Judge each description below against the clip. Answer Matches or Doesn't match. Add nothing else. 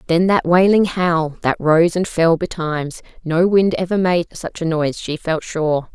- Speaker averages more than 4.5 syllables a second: Doesn't match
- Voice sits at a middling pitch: Matches